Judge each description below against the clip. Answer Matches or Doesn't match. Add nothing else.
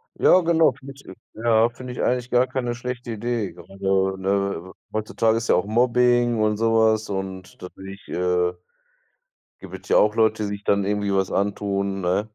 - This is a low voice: Matches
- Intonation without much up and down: Doesn't match